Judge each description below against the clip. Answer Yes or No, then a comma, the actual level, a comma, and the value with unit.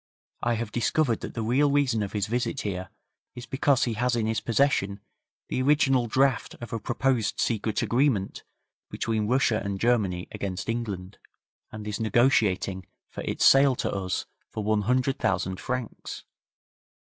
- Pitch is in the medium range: No, low, 115 Hz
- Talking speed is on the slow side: No, average, 155 wpm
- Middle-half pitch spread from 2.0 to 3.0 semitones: No, average, 3.7 semitones